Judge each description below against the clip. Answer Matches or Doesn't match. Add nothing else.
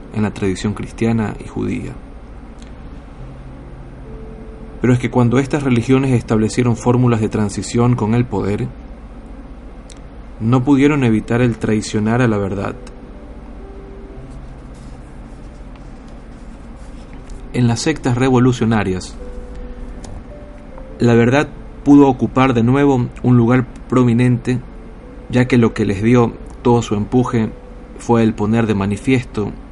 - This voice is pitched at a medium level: Doesn't match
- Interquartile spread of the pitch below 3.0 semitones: Matches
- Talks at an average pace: Doesn't match